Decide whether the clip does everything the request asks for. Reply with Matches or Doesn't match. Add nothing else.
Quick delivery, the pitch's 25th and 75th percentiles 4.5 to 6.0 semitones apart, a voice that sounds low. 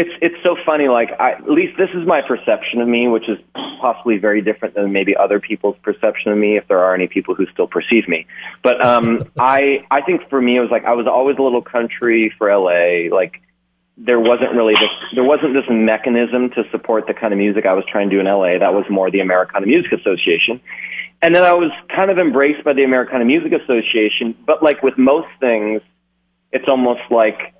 Matches